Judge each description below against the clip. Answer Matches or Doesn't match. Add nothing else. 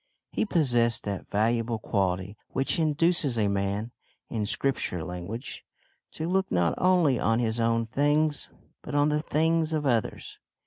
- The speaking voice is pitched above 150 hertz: Doesn't match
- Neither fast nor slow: Matches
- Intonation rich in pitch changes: Matches